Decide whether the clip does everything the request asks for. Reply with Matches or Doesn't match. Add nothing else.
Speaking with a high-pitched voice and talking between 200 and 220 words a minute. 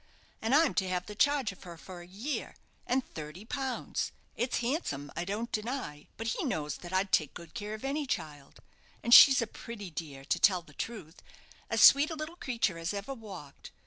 Matches